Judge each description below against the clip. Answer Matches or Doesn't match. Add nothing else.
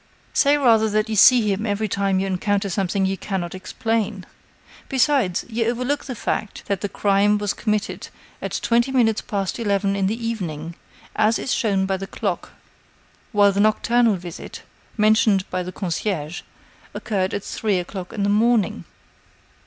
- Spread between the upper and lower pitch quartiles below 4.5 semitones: Matches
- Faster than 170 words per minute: Doesn't match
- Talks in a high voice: Matches